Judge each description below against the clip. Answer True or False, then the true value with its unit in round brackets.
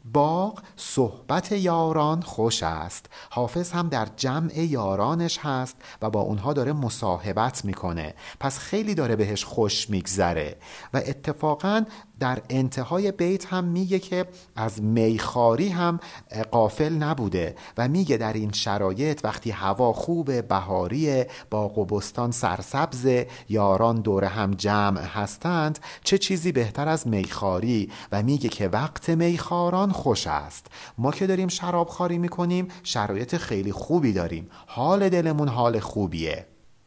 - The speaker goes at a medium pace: True (130 wpm)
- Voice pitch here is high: False (130 Hz)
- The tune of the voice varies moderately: False (8.3 semitones)